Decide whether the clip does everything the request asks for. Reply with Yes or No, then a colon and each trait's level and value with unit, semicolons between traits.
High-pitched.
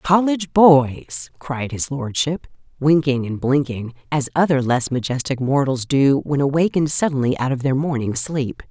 No: medium, 140 Hz